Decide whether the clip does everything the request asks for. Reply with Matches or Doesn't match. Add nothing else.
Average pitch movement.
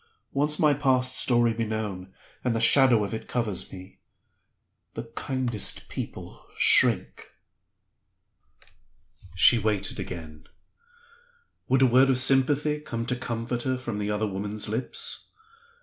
Matches